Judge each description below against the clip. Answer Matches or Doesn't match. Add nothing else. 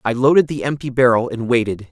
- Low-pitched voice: Matches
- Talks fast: Matches